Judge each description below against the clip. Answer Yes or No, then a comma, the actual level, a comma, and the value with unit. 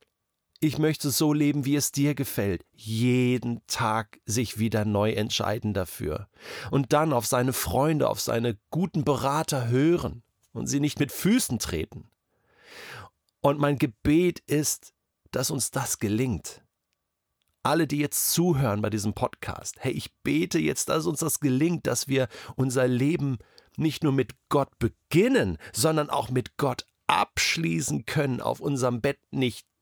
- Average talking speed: Yes, average, 145 wpm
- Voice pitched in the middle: No, low, 130 Hz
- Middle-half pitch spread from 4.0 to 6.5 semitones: Yes, average, 4.6 semitones